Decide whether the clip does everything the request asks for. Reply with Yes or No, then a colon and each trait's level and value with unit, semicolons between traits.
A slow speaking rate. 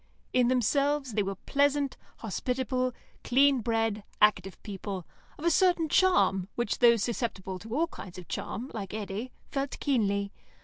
No: average, 145 wpm